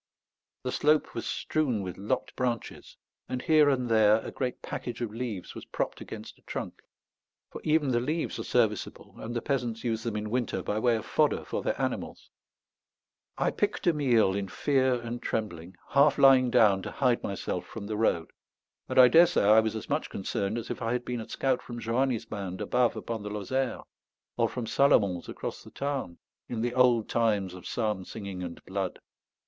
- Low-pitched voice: Yes, low, 115 Hz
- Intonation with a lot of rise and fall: No, average, 3.5 semitones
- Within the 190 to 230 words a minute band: Yes, average, 195 wpm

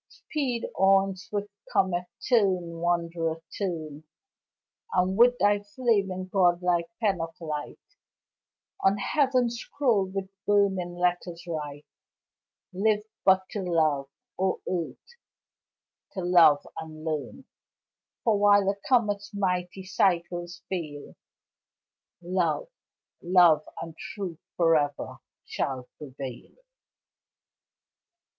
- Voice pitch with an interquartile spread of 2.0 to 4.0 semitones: Yes, average, 3.4 semitones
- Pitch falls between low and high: Yes, medium, 180 Hz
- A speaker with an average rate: No, slow, 100 wpm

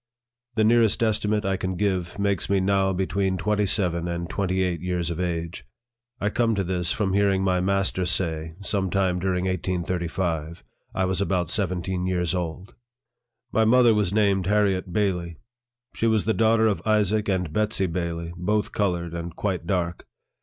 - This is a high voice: No, very low, 95 Hz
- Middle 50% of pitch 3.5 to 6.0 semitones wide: No, narrow, 2.6 semitones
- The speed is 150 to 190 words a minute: Yes, average, 170 wpm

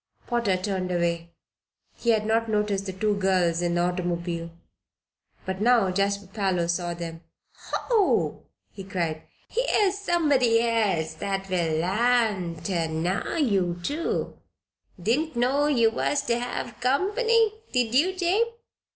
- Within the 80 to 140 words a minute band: Yes, slow, 135 wpm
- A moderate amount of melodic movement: No, wide, 6.1 semitones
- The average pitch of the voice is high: Yes, high, 205 Hz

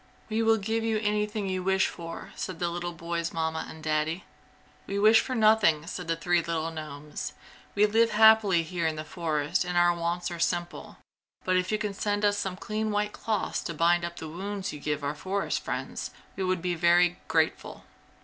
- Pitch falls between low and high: Yes, medium, 180 Hz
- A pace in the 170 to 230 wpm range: Yes, average, 200 wpm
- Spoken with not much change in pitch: No, average, 3.8 semitones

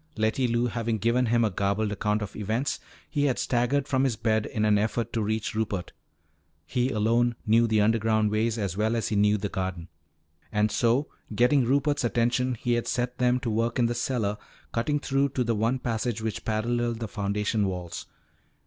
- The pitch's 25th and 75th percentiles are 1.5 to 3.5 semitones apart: Yes, narrow, 2.4 semitones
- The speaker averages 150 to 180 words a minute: No, average, 195 wpm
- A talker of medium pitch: No, low, 115 Hz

